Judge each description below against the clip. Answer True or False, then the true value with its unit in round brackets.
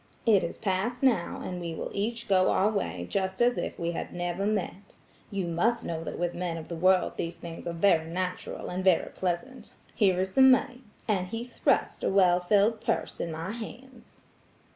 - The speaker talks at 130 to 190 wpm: False (200 wpm)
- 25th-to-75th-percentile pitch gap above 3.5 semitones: True (4.2 semitones)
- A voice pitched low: False (190 Hz)